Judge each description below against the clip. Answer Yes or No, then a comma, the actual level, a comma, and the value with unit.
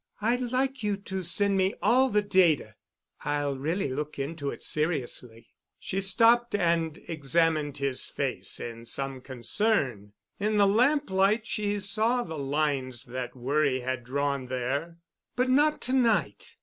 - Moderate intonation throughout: No, wide, 7.4 semitones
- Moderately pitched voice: Yes, medium, 165 Hz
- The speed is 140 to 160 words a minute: Yes, average, 145 wpm